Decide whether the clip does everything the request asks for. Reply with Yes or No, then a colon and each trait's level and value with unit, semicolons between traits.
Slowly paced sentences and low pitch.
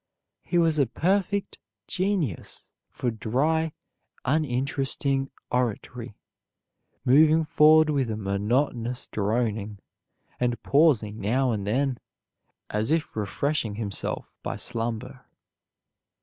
Yes: slow, 95 wpm; low, 125 Hz